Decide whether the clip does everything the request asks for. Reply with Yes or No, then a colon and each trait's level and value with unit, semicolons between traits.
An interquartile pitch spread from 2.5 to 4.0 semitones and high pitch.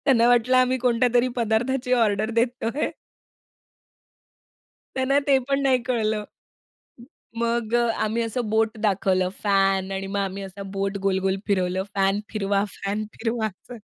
Yes: average, 3.6 semitones; high, 220 Hz